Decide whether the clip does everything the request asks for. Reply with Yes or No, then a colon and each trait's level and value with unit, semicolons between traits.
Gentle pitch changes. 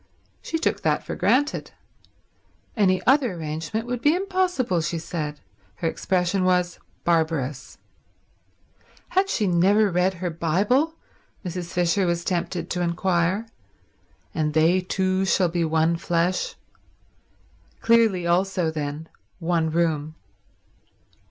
No: average, 3.1 semitones